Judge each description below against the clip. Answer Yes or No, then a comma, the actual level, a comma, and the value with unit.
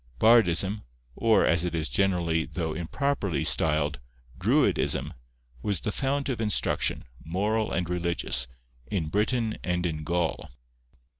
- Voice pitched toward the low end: Yes, very low, 90 Hz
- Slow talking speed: Yes, slow, 125 wpm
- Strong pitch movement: No, average, 4.8 semitones